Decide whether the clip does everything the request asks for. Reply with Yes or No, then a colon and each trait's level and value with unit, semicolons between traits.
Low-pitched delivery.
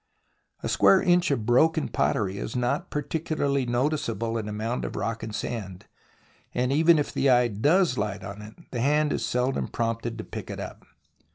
Yes: low, 120 Hz